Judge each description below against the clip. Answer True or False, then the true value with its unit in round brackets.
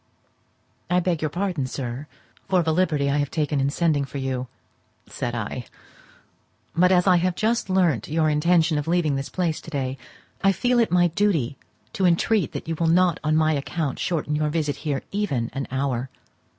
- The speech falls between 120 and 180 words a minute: False (190 wpm)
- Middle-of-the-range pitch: True (155 Hz)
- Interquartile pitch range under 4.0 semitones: False (4.3 semitones)